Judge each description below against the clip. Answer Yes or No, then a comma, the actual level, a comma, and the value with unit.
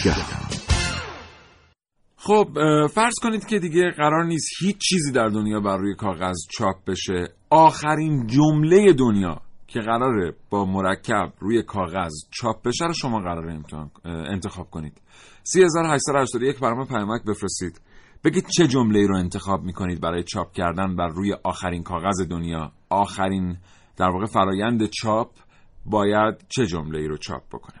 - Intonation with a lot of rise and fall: Yes, wide, 7.6 semitones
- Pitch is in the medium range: No, low, 100 Hz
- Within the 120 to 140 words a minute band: Yes, average, 135 wpm